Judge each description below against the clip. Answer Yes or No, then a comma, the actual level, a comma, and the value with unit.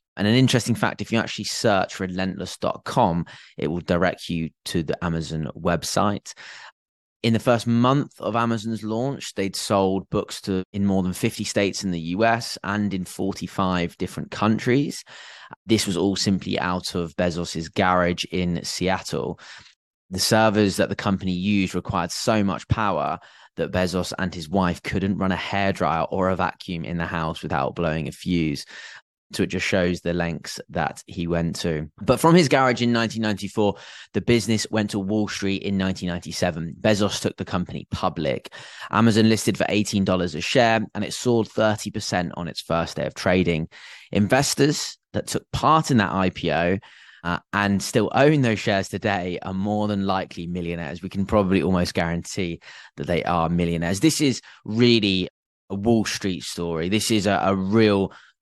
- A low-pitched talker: Yes, very low, 95 Hz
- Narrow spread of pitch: No, average, 3.7 semitones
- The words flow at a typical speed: Yes, average, 170 wpm